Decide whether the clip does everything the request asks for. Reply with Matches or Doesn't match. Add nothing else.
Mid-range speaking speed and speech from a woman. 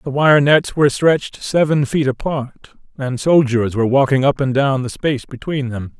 Doesn't match